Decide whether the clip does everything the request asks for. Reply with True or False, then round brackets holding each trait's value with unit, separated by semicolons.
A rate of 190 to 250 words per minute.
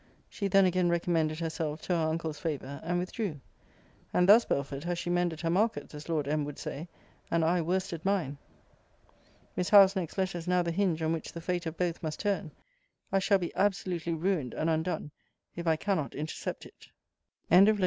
True (200 wpm)